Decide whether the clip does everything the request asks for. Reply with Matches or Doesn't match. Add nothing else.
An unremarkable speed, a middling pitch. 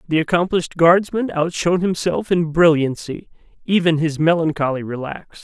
Doesn't match